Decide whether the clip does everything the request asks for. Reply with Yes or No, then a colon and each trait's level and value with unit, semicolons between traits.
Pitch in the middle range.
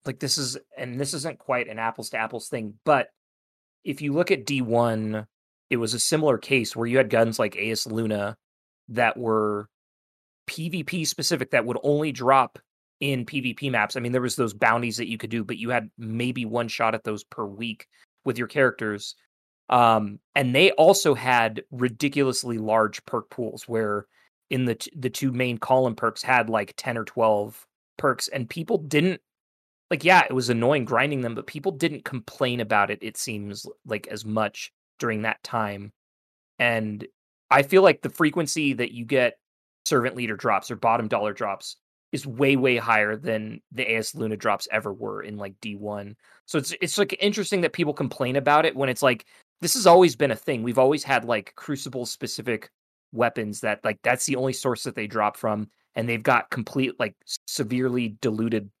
No: low, 120 Hz